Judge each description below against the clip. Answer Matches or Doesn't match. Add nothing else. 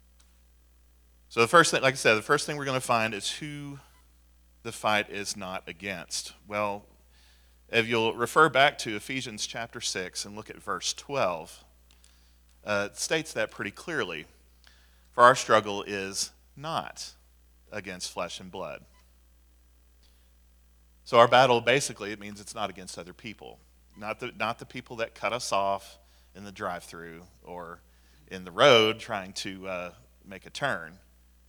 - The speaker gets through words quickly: Doesn't match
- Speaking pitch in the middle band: Doesn't match